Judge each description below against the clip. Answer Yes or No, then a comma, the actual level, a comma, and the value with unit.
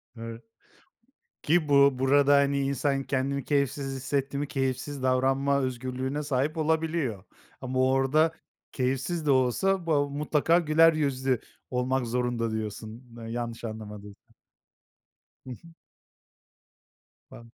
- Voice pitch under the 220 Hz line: Yes, low, 135 Hz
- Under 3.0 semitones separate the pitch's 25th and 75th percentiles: Yes, narrow, 2.4 semitones